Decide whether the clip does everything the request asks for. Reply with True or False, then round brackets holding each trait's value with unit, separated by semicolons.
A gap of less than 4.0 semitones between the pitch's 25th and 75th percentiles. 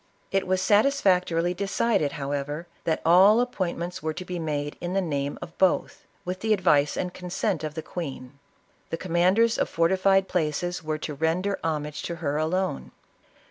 True (3.5 semitones)